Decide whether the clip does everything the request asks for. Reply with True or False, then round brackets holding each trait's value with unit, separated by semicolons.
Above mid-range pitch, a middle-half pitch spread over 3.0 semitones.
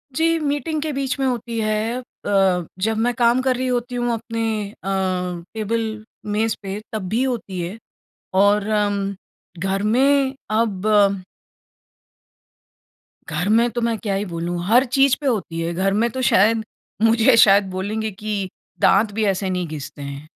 True (215 Hz; 3.6 semitones)